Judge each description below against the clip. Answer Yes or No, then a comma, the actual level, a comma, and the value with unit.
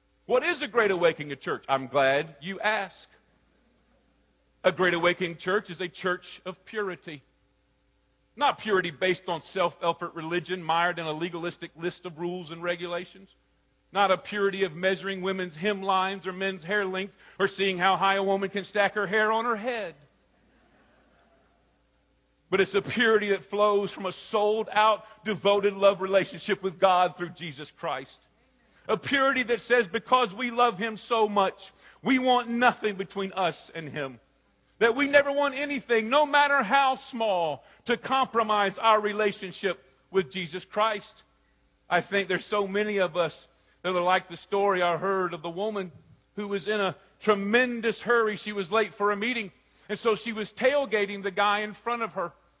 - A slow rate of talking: No, average, 170 wpm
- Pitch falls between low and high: No, high, 195 Hz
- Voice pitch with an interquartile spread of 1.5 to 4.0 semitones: Yes, average, 3.4 semitones